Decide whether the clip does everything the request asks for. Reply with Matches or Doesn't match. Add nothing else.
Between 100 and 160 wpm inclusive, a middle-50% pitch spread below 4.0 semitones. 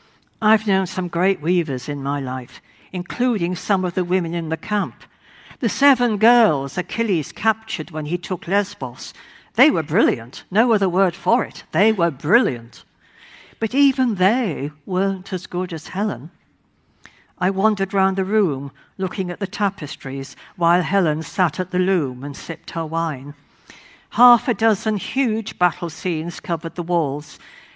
Doesn't match